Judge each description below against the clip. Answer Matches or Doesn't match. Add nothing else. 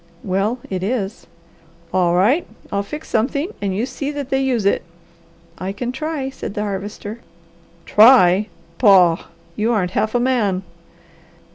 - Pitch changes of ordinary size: Matches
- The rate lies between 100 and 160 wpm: Matches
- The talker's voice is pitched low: Doesn't match